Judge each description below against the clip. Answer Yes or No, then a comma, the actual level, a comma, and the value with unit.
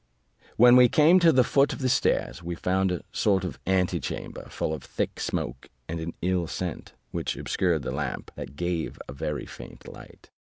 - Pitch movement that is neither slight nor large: No, wide, 7.0 semitones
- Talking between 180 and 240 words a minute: Yes, average, 190 wpm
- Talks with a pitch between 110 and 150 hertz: No, very low, 90 Hz